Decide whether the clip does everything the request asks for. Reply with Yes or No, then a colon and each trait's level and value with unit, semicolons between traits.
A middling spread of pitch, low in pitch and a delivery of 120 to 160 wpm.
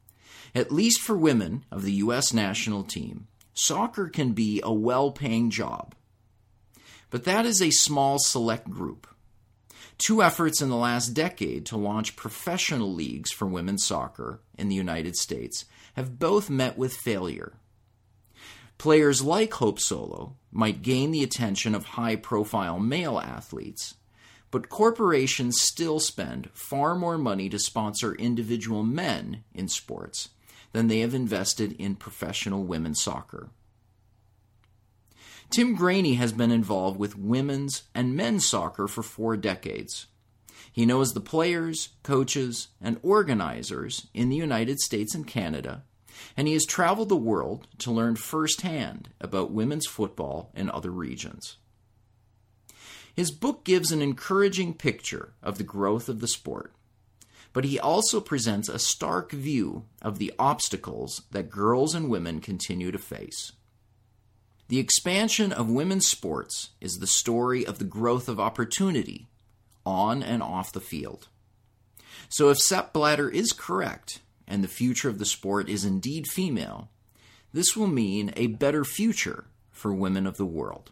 Yes: average, 4.9 semitones; low, 115 Hz; average, 145 wpm